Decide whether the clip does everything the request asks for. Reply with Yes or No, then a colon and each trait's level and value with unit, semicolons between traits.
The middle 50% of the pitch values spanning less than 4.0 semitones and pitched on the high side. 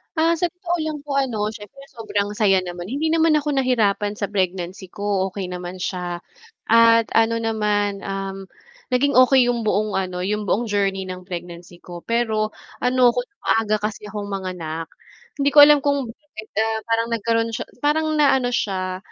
No: average, 4.7 semitones; high, 215 Hz